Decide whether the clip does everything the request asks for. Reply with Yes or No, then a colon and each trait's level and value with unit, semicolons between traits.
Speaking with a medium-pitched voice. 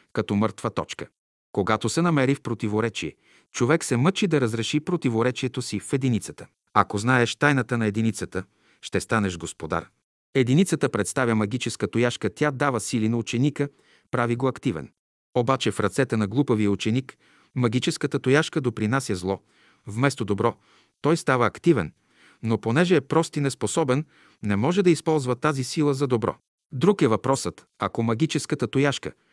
No: low, 125 Hz